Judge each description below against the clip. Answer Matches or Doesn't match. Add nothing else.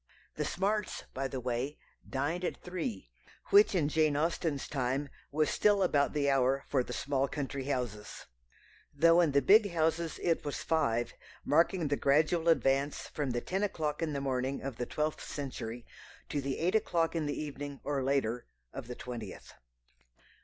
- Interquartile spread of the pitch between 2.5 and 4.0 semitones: Matches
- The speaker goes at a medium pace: Matches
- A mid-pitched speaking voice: Matches